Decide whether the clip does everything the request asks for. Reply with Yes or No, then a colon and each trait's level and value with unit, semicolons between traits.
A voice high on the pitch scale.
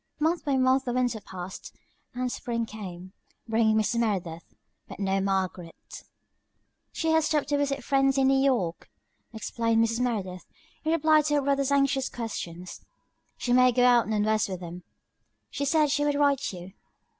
Yes: high, 245 Hz